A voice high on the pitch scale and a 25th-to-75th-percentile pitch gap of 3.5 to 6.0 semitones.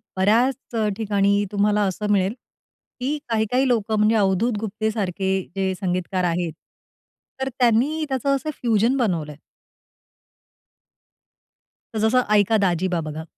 Yes: high, 210 Hz; average, 4.1 semitones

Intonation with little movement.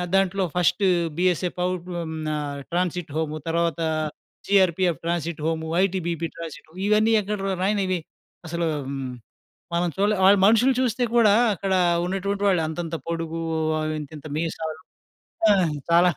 No: average, 3.1 semitones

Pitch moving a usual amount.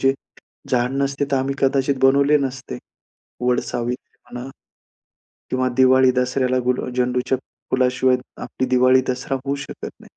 No: narrow, 1.1 semitones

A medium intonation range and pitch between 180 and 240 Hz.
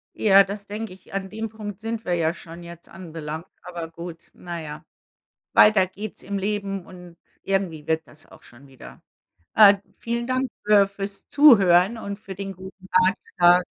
Yes: average, 3.2 semitones; high, 190 Hz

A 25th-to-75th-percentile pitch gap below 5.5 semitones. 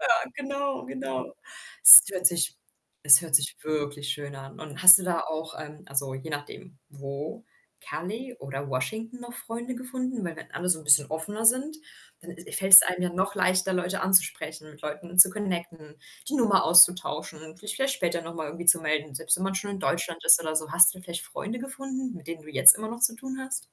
No: wide, 5.8 semitones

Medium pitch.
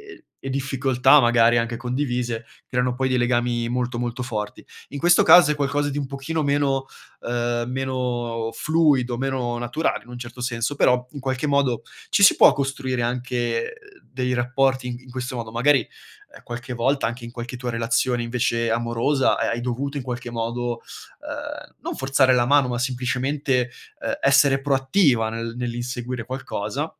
No: low, 125 Hz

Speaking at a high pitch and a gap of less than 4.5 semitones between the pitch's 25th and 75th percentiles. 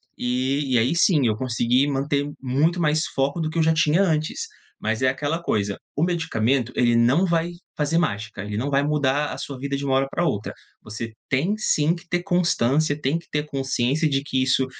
No: medium, 140 Hz; average, 3.9 semitones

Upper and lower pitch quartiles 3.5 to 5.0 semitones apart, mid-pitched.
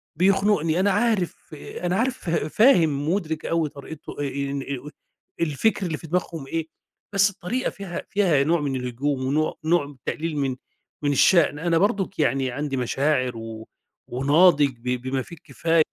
Yes: average, 4.5 semitones; medium, 155 Hz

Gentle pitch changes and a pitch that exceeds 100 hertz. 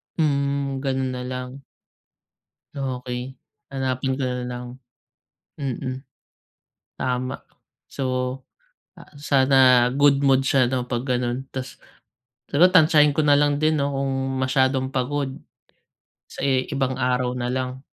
Yes: narrow, 1.6 semitones; low, 130 Hz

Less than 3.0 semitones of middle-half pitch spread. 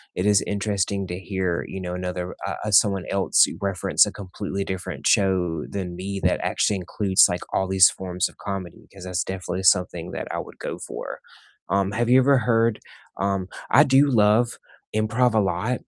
Yes: narrow, 2.6 semitones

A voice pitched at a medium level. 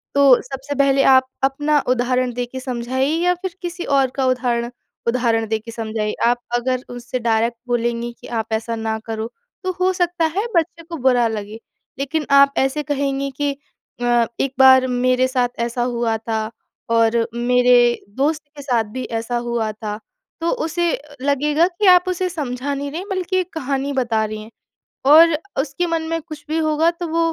No: very high, 260 Hz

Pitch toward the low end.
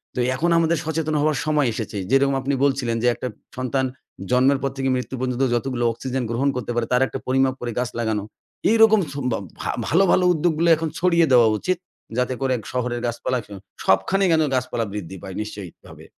Yes: low, 130 Hz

